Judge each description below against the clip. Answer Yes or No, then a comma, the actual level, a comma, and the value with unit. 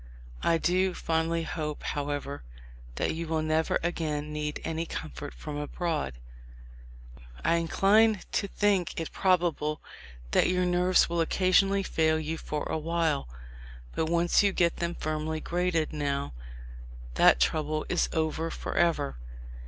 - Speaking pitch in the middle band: Yes, medium, 160 Hz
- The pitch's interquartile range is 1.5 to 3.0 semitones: Yes, narrow, 2.5 semitones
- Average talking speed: No, slow, 130 wpm